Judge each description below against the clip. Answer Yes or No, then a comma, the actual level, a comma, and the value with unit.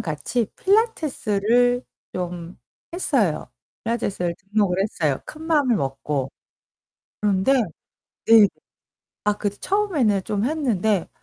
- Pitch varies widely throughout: Yes, wide, 5.8 semitones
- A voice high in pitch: Yes, high, 210 Hz